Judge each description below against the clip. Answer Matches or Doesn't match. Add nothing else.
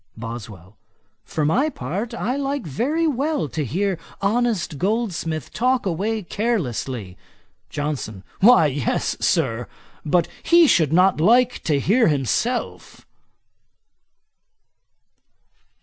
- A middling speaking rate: Doesn't match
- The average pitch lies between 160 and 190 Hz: Matches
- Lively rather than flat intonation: Matches